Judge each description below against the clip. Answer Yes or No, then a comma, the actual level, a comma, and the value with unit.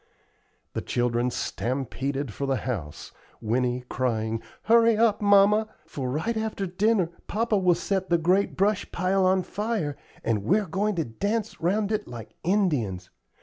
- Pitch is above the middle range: No, medium, 180 Hz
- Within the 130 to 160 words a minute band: Yes, average, 145 wpm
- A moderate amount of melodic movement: No, wide, 8.7 semitones